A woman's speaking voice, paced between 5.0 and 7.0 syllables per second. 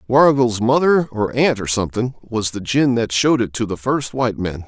No: male; 5.4 syllables/s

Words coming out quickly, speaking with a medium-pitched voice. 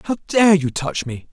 Yes: fast, 225 wpm; medium, 165 Hz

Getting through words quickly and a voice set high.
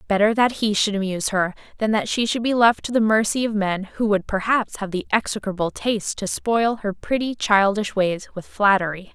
Yes: fast, 210 wpm; high, 210 Hz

